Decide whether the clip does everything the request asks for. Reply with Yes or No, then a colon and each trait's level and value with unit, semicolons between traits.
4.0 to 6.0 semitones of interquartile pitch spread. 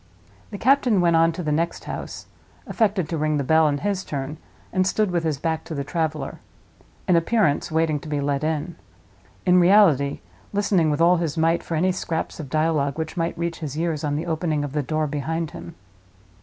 No: narrow, 2.6 semitones